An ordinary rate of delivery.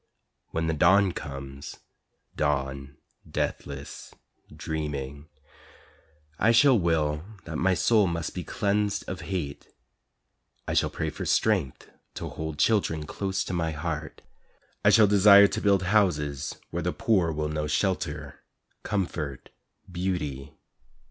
No: slow, 125 wpm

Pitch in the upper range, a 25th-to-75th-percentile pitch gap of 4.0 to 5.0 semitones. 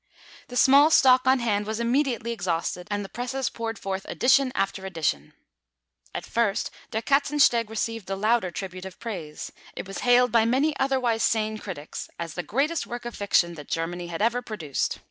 Yes: high, 225 Hz; average, 4.6 semitones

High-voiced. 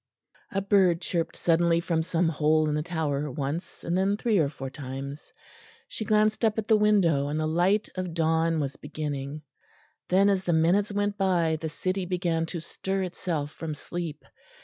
No: medium, 170 Hz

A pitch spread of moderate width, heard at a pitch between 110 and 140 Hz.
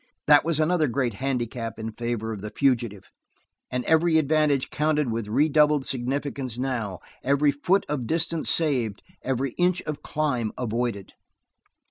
Yes: average, 4.3 semitones; low, 135 Hz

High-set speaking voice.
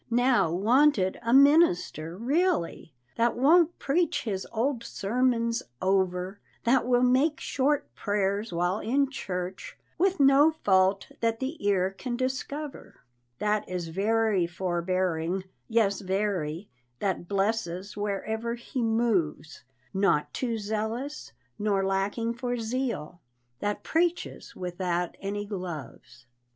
Yes: high, 210 Hz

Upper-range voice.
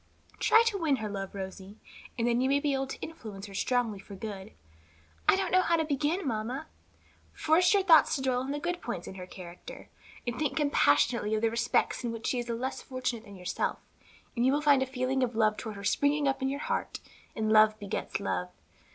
Yes: high, 245 Hz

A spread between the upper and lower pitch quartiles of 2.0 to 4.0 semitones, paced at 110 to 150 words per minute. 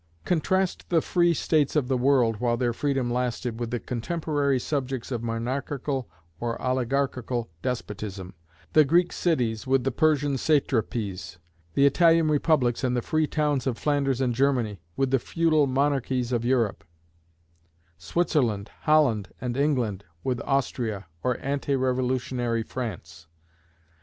Yes: average, 3.4 semitones; slow, 135 wpm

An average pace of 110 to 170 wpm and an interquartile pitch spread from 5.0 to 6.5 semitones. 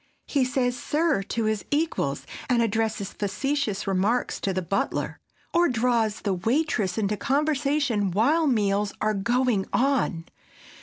Yes: slow, 135 wpm; wide, 5.4 semitones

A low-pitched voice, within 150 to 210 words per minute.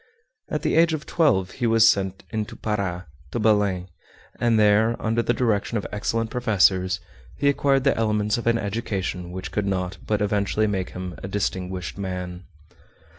Yes: low, 105 Hz; average, 170 wpm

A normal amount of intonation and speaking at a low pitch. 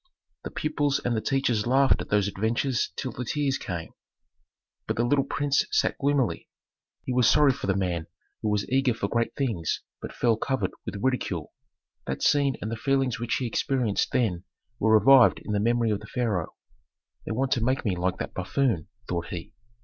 Yes: average, 4.7 semitones; low, 120 Hz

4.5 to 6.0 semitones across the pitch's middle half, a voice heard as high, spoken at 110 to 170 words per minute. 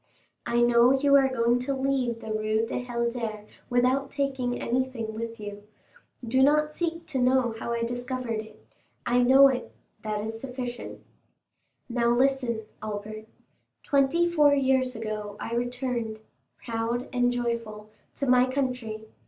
No: narrow, 2.6 semitones; high, 245 Hz; average, 140 wpm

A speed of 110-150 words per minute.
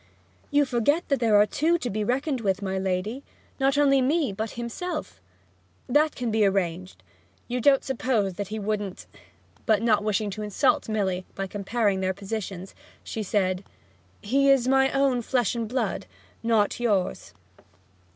No: average, 160 wpm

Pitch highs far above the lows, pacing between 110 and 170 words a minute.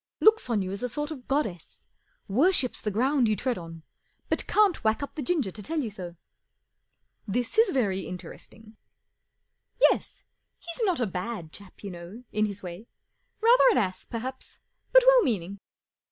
No: wide, 7.3 semitones; average, 180 wpm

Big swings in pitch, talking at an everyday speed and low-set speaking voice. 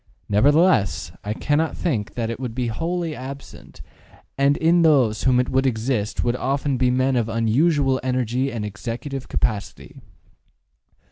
No: average, 3.4 semitones; average, 145 wpm; low, 130 Hz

